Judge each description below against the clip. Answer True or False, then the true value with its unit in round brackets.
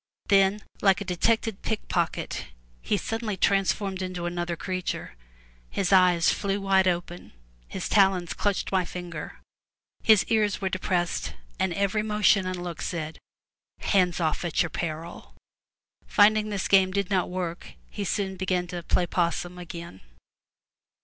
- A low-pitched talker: False (185 Hz)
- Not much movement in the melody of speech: True (2.2 semitones)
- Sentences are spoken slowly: False (145 wpm)